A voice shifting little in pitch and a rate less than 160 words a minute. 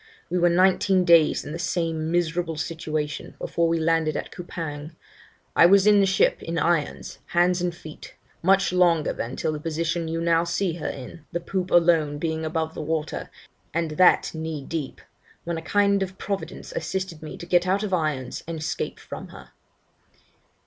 No: narrow, 2.1 semitones; average, 175 wpm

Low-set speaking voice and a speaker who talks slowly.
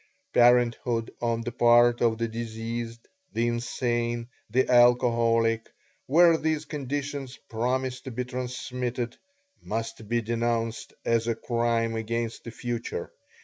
Yes: low, 120 Hz; slow, 120 wpm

